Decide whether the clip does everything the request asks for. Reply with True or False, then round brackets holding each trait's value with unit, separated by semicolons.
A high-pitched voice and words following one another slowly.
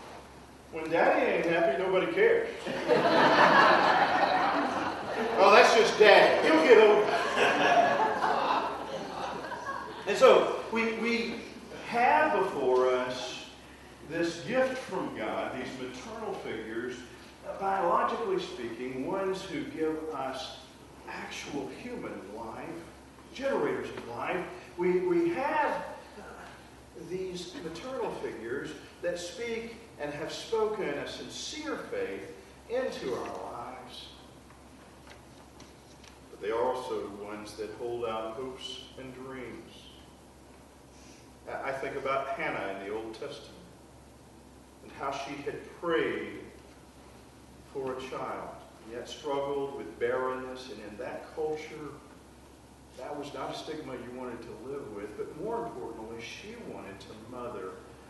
False (150 Hz; 115 wpm)